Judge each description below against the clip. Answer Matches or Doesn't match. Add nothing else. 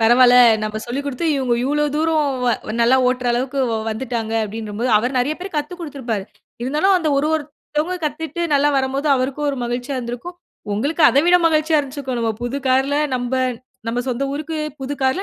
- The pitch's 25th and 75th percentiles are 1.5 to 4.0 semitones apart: Matches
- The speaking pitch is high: Matches